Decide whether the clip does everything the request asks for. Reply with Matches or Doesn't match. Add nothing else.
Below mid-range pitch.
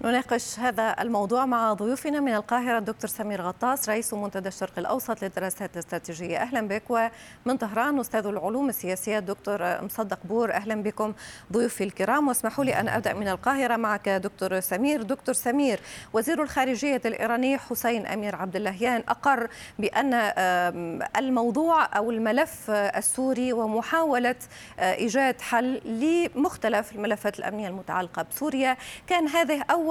Doesn't match